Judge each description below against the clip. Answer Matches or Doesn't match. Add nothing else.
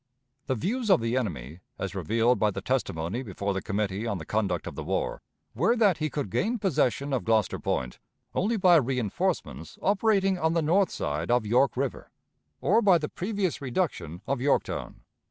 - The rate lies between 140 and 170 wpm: Doesn't match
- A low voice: Matches